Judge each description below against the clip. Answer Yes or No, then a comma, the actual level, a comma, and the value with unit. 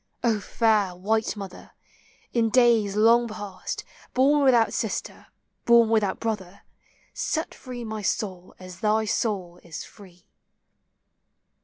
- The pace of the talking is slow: Yes, slow, 120 wpm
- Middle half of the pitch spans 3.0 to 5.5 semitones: Yes, average, 3.4 semitones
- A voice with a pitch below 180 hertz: No, high, 215 Hz